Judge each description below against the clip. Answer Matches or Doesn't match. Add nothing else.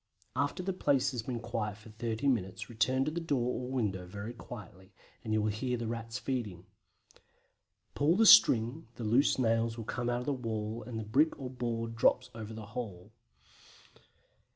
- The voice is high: Doesn't match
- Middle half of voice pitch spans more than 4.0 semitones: Doesn't match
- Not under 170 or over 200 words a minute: Matches